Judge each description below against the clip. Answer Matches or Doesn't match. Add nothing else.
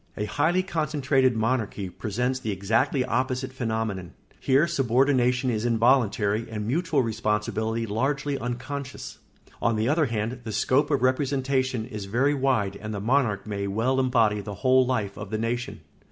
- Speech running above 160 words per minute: Doesn't match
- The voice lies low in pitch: Matches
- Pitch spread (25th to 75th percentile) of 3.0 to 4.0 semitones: Matches